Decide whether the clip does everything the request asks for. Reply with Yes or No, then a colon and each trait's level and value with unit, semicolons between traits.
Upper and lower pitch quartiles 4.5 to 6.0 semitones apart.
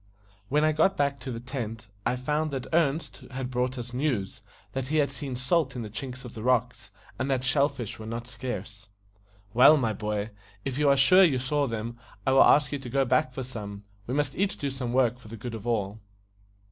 No: average, 3.2 semitones